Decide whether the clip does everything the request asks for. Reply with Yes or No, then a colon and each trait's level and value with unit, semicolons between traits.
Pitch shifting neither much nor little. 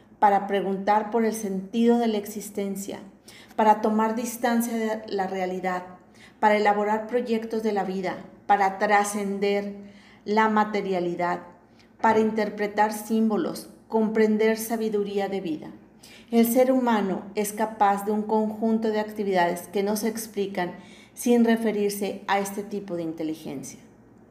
No: narrow, 2.1 semitones